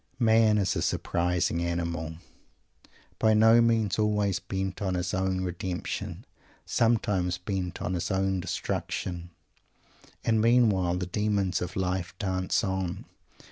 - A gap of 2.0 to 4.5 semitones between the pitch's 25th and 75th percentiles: Yes, average, 2.7 semitones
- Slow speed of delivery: Yes, slow, 125 wpm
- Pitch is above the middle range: No, very low, 95 Hz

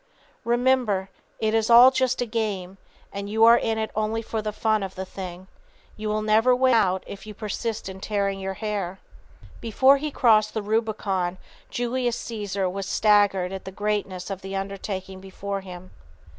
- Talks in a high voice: Yes, high, 210 Hz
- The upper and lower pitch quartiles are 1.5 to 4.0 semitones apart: Yes, average, 2.7 semitones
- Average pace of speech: Yes, average, 175 wpm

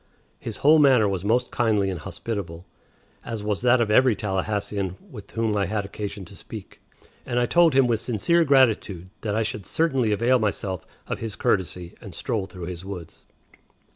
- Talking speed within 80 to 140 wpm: No, average, 180 wpm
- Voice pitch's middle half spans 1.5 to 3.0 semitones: No, average, 3.9 semitones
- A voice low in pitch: Yes, low, 105 Hz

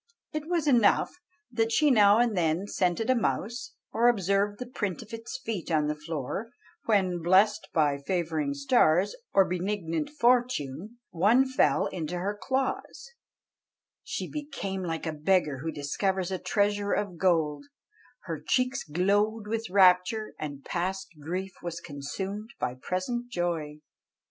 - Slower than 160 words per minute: Yes, average, 145 wpm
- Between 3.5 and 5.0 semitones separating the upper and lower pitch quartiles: No, wide, 5.4 semitones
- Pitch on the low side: No, high, 190 Hz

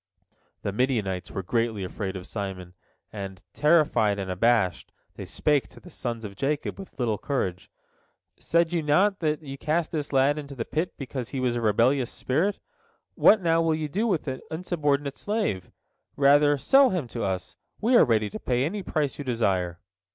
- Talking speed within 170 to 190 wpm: Yes, average, 185 wpm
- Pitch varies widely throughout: Yes, wide, 6.7 semitones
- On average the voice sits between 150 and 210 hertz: No, low, 135 Hz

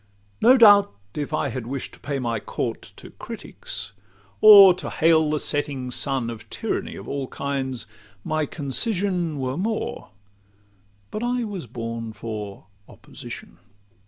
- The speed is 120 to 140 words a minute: Yes, slow, 135 wpm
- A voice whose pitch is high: No, low, 135 Hz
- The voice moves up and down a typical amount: No, wide, 7.7 semitones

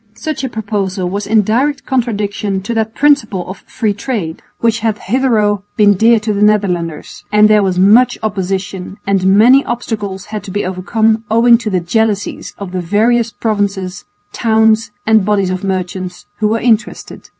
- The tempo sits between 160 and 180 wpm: Yes, average, 170 wpm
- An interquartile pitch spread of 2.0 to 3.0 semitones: Yes, average, 2.7 semitones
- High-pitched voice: Yes, high, 210 Hz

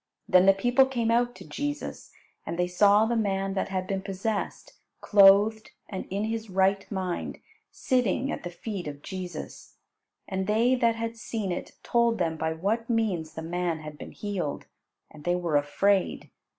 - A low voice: No, high, 195 Hz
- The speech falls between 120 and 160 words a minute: No, average, 175 wpm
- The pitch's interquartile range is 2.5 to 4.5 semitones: Yes, average, 4.1 semitones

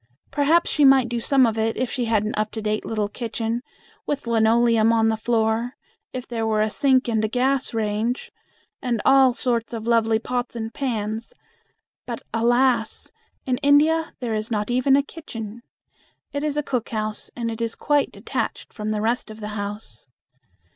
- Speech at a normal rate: Yes, average, 180 wpm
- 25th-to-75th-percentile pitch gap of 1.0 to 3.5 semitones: Yes, narrow, 2.6 semitones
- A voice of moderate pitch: No, high, 230 Hz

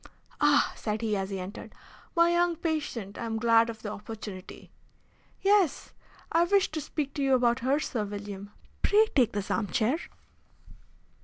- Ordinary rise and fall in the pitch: No, wide, 6.9 semitones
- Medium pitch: No, high, 235 Hz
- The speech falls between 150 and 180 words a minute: Yes, average, 165 wpm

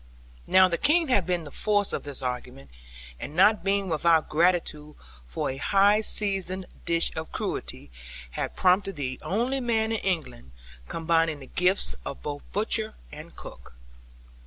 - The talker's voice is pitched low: No, medium, 175 Hz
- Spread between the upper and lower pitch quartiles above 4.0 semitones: Yes, wide, 5.4 semitones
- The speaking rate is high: No, average, 155 wpm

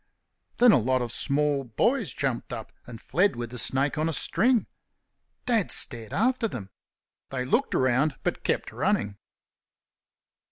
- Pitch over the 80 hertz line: Yes, low, 135 Hz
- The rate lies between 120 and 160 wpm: Yes, average, 150 wpm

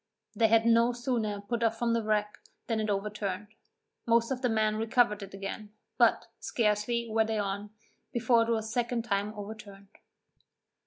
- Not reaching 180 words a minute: Yes, average, 170 wpm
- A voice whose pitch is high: Yes, high, 220 Hz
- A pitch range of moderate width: No, narrow, 2.0 semitones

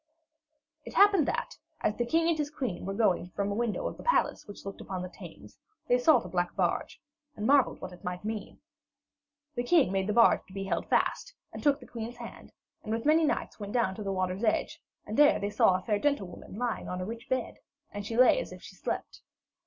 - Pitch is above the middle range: Yes, high, 225 Hz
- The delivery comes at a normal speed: No, fast, 230 wpm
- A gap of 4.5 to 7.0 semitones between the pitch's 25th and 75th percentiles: Yes, average, 5.1 semitones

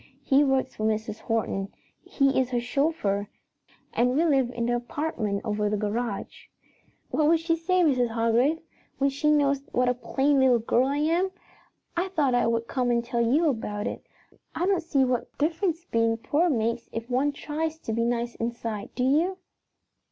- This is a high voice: Yes, very high, 250 Hz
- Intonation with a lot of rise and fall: No, average, 4.6 semitones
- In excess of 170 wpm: Yes, average, 180 wpm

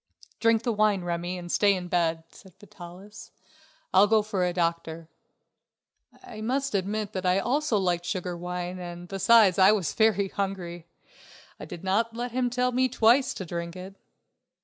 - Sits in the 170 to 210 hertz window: Yes, high, 190 Hz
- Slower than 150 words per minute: No, average, 170 wpm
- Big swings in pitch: No, average, 3.8 semitones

